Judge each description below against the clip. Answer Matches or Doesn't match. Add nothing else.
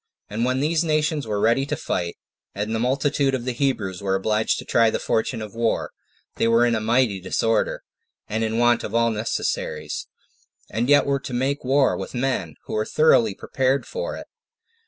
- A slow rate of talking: Doesn't match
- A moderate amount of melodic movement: Matches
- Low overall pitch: Matches